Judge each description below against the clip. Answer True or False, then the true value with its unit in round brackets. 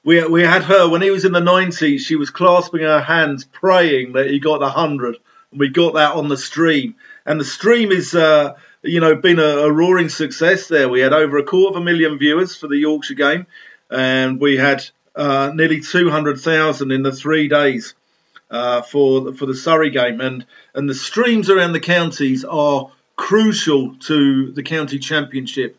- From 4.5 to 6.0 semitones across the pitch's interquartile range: False (3.9 semitones)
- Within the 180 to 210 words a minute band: True (195 wpm)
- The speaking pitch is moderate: True (155 Hz)